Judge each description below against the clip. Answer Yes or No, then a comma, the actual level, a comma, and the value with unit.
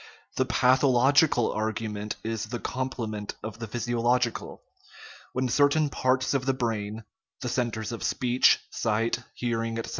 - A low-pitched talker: Yes, low, 120 Hz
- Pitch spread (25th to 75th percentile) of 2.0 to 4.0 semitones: Yes, narrow, 2.6 semitones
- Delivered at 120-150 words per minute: Yes, average, 140 wpm